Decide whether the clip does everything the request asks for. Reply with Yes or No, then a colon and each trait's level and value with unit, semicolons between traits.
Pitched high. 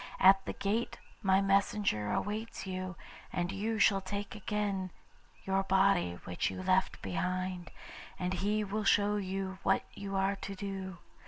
Yes: high, 195 Hz